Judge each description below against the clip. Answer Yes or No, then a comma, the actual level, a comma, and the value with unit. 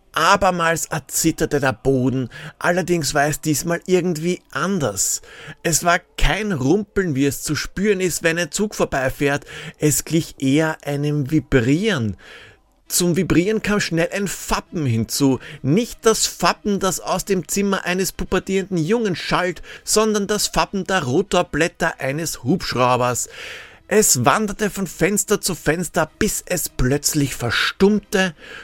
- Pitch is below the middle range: No, medium, 165 Hz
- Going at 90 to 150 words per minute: Yes, average, 130 wpm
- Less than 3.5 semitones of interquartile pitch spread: No, average, 4.7 semitones